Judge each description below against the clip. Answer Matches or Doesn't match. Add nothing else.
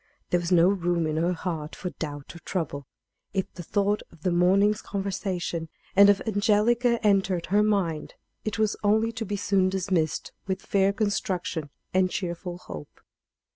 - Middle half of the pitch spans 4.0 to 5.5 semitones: Doesn't match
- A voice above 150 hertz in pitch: Matches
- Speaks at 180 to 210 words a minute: Doesn't match